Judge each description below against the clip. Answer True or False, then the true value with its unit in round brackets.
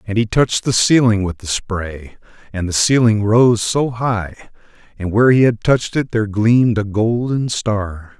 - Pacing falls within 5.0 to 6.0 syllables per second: False (4.7 syllables/s)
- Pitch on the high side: False (110 Hz)